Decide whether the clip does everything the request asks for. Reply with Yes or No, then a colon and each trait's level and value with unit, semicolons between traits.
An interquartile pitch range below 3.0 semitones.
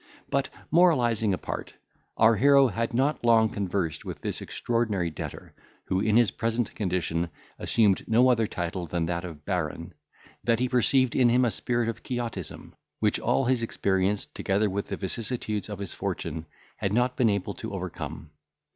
No: average, 4.4 semitones